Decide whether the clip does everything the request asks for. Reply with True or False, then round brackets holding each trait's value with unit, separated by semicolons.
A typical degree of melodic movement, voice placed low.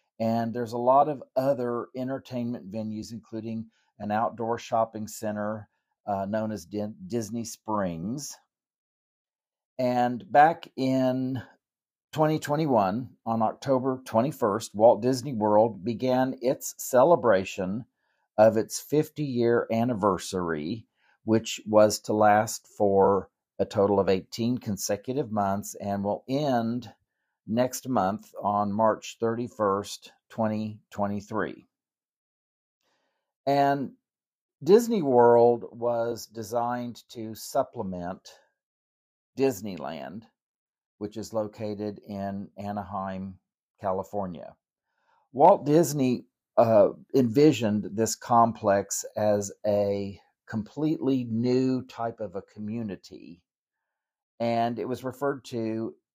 True (3.2 semitones; 115 Hz)